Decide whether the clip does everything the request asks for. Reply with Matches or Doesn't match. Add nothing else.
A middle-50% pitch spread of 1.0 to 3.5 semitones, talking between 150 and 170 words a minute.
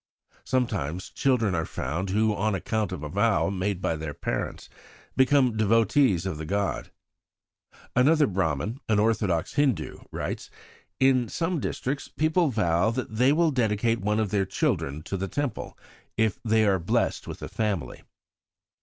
Doesn't match